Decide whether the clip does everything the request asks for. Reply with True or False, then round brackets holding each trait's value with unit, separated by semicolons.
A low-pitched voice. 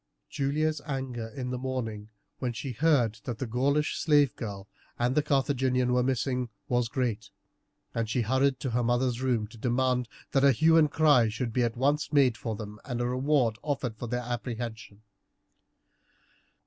True (125 Hz)